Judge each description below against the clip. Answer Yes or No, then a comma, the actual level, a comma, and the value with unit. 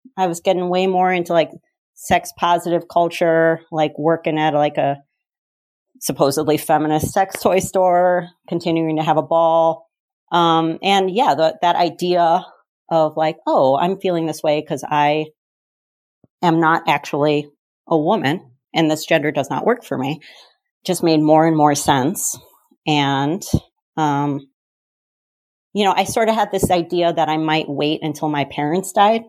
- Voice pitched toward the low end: No, medium, 165 Hz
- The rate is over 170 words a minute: No, average, 160 wpm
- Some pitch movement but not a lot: Yes, average, 3.0 semitones